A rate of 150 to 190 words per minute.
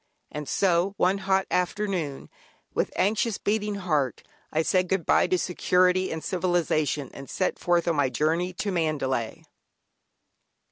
No: average, 140 wpm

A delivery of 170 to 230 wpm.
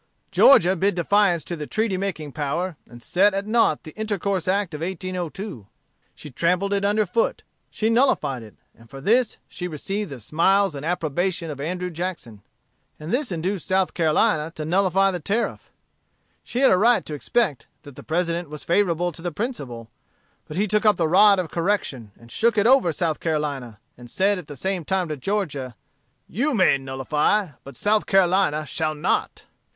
Yes: average, 180 wpm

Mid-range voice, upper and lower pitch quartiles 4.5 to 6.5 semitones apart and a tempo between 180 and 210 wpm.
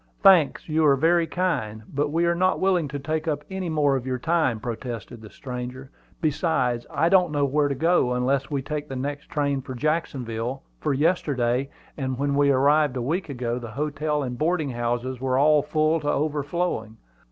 No: medium, 145 Hz; average, 3.5 semitones; average, 190 wpm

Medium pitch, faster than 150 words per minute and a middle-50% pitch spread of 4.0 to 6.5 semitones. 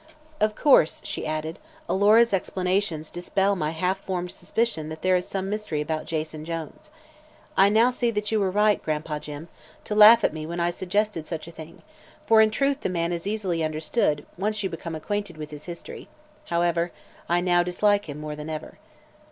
Yes: medium, 175 Hz; average, 190 wpm; average, 4.6 semitones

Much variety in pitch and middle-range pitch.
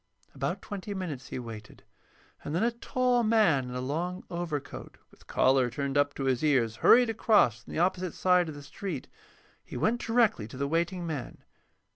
Yes: wide, 6.7 semitones; medium, 160 Hz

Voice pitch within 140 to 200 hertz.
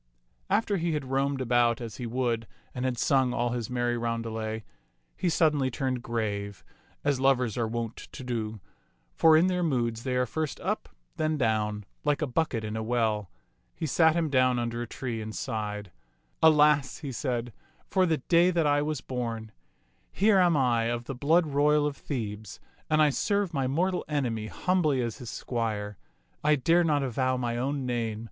No: low, 130 Hz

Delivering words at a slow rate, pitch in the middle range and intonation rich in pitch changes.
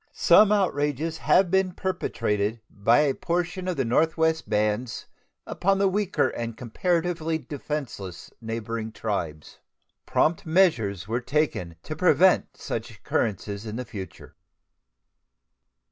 Yes: slow, 115 wpm; medium, 145 Hz; wide, 8.0 semitones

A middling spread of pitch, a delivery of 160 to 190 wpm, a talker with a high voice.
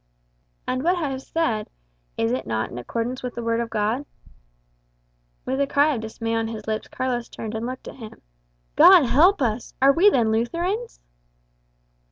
Yes: average, 4.1 semitones; average, 180 wpm; high, 240 Hz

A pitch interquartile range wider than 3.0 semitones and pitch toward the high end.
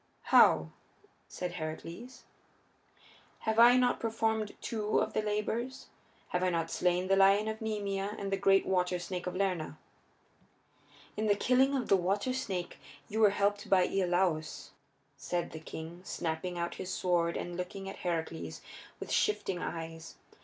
Yes: average, 3.4 semitones; high, 195 Hz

